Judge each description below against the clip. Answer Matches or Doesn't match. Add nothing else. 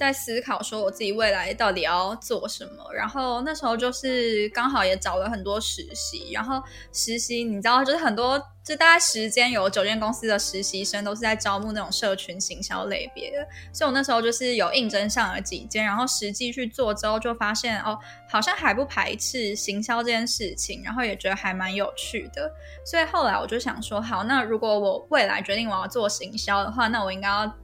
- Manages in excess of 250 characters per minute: Matches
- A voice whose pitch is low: Doesn't match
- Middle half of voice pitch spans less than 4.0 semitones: Matches